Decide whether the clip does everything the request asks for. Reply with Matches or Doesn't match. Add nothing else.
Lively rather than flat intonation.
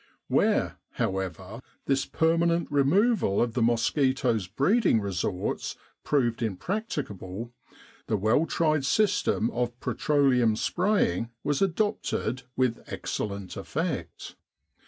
Matches